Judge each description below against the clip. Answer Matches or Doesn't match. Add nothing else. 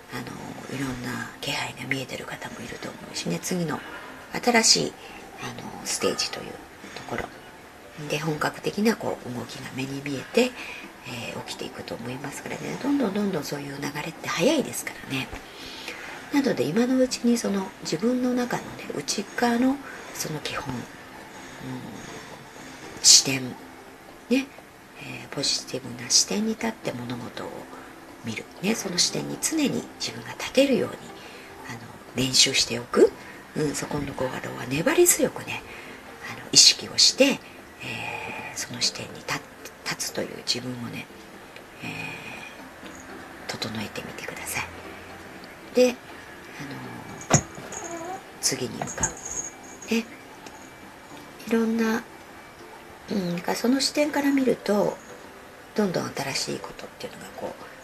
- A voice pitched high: Matches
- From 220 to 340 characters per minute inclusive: Matches